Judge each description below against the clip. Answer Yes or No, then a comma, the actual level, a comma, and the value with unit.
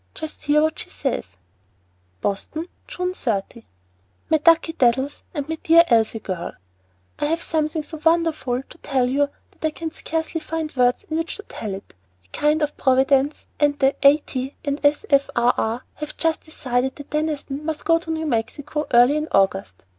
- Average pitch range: Yes, average, 4.0 semitones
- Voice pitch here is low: No, very high, 290 Hz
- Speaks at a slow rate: No, average, 175 wpm